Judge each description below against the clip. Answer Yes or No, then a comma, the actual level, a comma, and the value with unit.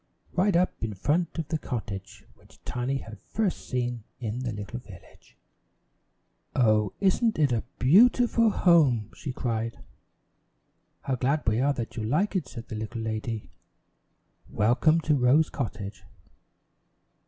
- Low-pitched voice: Yes, low, 125 Hz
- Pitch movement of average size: No, wide, 6.1 semitones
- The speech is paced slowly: No, average, 145 wpm